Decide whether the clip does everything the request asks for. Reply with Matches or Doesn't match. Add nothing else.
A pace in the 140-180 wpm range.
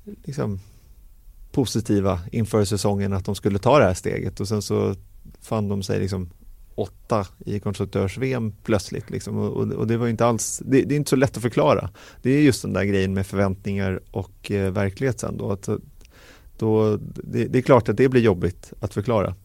Doesn't match